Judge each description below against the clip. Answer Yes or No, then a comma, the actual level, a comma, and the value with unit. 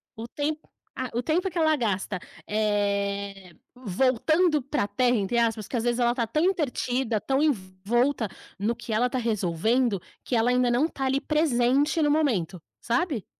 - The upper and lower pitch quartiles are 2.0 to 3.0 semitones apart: No, average, 5.0 semitones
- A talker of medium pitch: No, high, 240 Hz